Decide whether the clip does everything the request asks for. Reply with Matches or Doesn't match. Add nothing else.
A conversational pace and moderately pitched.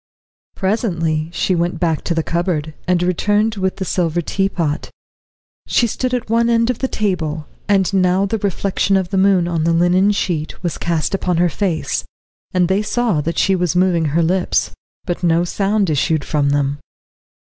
Matches